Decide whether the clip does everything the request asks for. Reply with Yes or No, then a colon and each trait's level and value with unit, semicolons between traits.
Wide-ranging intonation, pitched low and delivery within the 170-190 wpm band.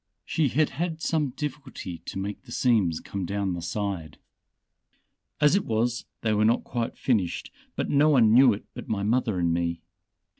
Yes: wide, 5.8 semitones; low, 110 Hz; average, 180 wpm